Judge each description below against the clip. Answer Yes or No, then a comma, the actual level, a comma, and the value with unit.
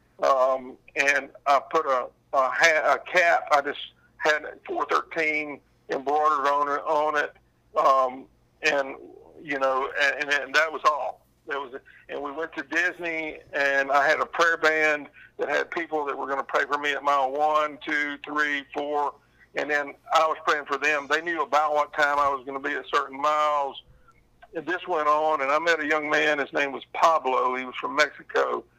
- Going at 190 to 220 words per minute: Yes, average, 200 wpm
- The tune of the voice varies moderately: No, narrow, 1.7 semitones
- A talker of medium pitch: Yes, medium, 150 Hz